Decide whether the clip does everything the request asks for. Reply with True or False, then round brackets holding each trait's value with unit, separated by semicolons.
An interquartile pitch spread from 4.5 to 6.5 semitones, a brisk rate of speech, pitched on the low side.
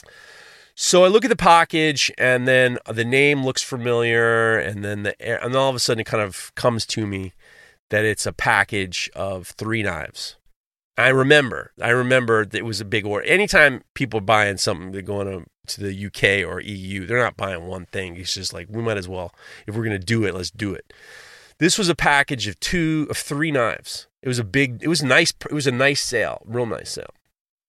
True (5.1 semitones; 220 wpm; 115 Hz)